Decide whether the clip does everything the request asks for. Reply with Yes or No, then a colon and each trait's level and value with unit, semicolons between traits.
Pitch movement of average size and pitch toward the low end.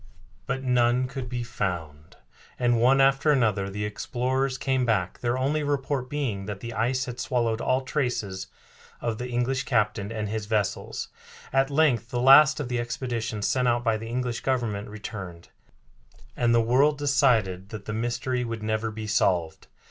Yes: average, 3.3 semitones; low, 120 Hz